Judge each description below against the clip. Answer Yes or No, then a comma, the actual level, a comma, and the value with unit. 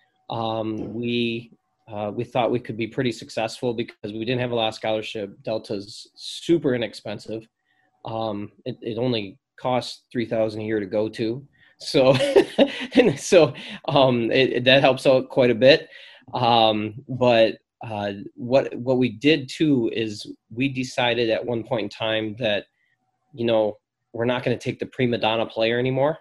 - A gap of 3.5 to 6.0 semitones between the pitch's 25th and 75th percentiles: No, average, 2.9 semitones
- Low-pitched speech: Yes, low, 120 Hz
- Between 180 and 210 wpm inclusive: No, average, 170 wpm